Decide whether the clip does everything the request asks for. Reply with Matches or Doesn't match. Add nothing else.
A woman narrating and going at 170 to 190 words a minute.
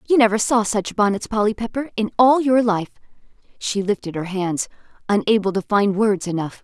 Matches